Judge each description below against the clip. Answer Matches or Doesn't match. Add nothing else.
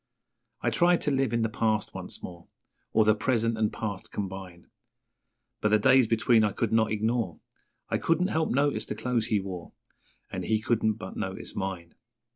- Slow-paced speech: Doesn't match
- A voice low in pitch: Matches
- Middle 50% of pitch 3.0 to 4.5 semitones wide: Doesn't match